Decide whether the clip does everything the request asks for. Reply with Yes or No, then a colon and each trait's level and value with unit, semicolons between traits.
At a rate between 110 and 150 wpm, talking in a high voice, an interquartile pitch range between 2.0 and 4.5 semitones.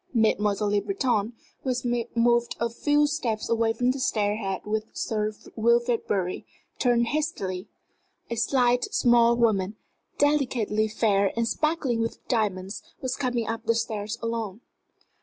Yes: average, 140 wpm; high, 230 Hz; narrow, 2.5 semitones